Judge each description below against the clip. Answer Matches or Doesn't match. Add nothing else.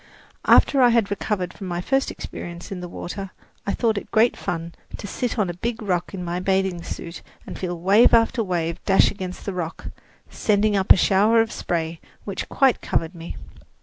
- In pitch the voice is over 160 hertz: Matches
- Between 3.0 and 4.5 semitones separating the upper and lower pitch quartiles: Matches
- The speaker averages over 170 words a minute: Matches